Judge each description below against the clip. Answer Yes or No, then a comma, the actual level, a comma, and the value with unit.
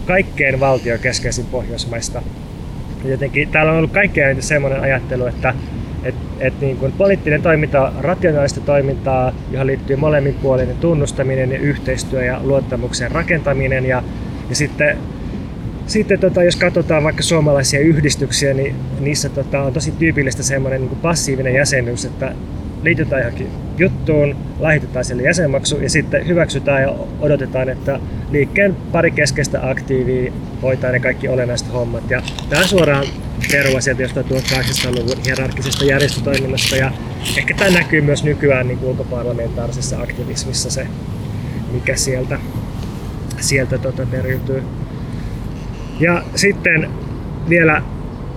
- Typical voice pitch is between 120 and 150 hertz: Yes, low, 135 Hz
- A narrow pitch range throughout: Yes, narrow, 2.3 semitones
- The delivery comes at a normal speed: Yes, average, 125 wpm